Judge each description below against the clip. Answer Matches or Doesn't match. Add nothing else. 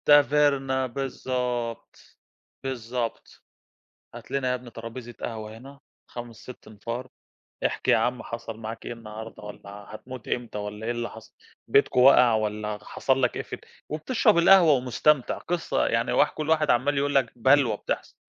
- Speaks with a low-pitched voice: Matches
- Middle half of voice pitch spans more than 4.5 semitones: Doesn't match